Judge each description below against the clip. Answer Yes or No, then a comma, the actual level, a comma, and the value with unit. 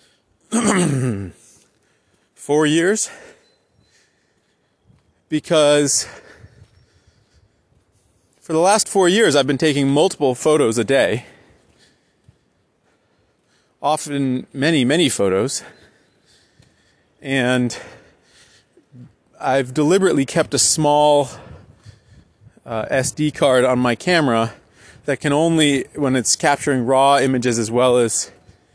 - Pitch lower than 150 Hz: Yes, low, 135 Hz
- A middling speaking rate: No, slow, 90 wpm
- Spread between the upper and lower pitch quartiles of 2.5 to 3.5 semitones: No, average, 4.9 semitones